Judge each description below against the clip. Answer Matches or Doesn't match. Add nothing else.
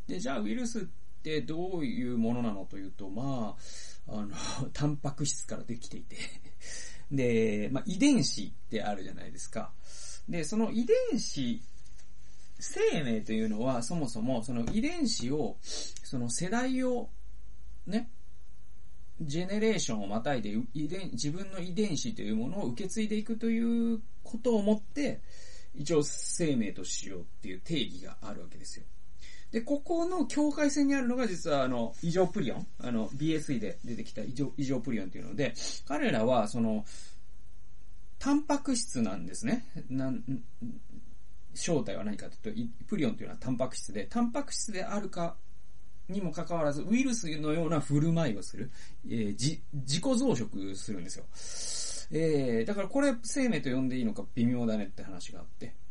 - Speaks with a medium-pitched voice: Matches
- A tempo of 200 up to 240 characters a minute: Doesn't match